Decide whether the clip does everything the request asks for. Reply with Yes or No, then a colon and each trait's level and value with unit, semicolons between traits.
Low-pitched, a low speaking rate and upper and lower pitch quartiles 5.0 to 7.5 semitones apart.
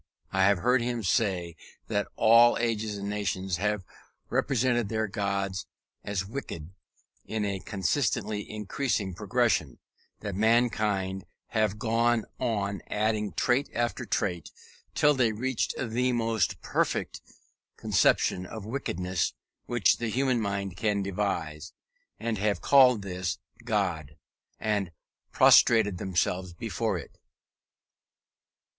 No: low, 105 Hz; slow, 120 wpm; average, 3.3 semitones